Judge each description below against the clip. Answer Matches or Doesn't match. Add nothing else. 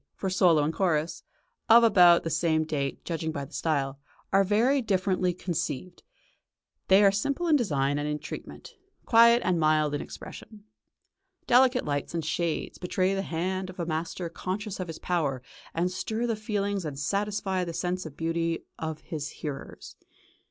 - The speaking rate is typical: Matches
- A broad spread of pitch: Doesn't match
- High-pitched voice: Doesn't match